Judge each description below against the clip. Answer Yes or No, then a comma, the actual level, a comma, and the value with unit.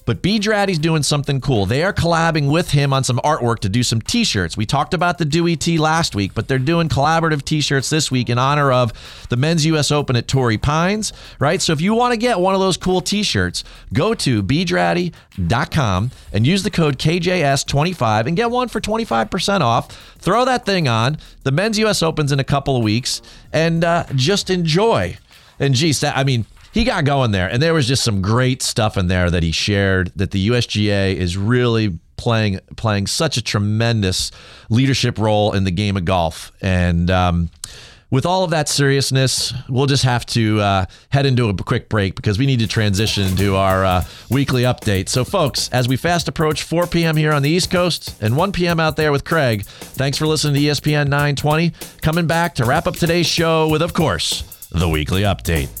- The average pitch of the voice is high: No, low, 135 Hz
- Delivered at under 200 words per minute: No, fast, 205 wpm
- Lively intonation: Yes, wide, 7.2 semitones